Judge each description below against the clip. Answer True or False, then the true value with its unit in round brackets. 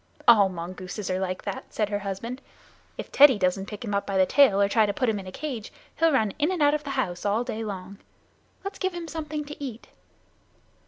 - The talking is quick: True (230 wpm)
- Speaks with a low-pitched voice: False (215 Hz)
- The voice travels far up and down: True (6.5 semitones)